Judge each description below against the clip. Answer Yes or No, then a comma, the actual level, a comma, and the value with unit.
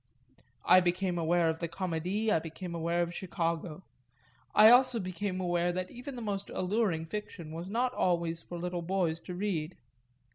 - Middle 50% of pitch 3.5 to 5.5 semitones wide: No, average, 2.8 semitones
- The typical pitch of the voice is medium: Yes, medium, 180 Hz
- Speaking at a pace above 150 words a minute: Yes, average, 170 wpm